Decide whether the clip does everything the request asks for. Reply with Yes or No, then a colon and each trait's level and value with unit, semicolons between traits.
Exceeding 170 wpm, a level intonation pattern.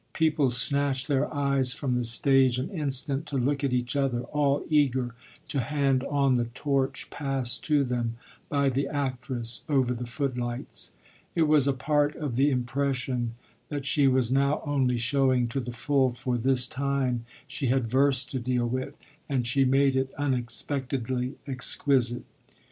No: average, 160 wpm; narrow, 2.2 semitones